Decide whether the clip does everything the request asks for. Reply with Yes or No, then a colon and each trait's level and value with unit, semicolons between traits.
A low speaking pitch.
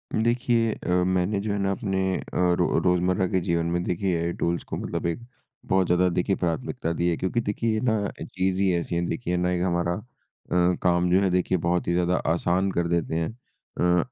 Yes: very low, 90 Hz